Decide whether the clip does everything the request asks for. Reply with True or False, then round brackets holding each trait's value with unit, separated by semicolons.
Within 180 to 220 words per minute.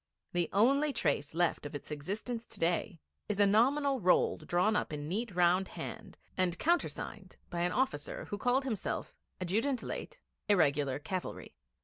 False (155 wpm)